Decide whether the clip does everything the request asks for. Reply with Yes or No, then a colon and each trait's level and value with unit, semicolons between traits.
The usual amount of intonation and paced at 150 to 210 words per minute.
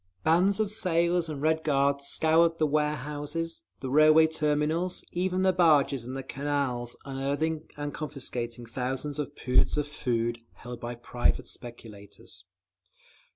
No: average, 4.0 semitones; slow, 135 wpm